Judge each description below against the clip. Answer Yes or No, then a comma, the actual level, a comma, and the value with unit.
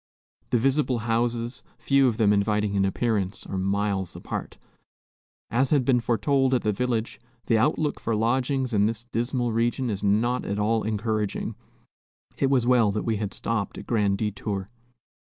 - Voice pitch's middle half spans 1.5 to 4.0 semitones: Yes, average, 3.1 semitones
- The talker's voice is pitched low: Yes, low, 115 Hz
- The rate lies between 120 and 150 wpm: No, average, 165 wpm